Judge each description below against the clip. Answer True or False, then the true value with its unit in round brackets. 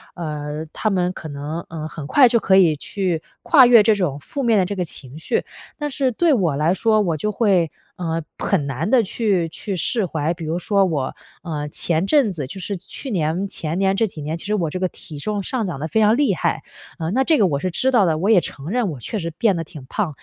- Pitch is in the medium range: True (180 Hz)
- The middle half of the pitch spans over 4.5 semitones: True (5.1 semitones)